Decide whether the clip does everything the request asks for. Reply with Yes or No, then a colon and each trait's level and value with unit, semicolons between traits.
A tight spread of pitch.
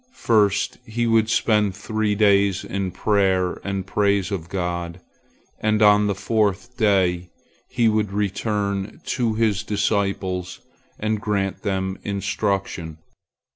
Yes: narrow, 2.0 semitones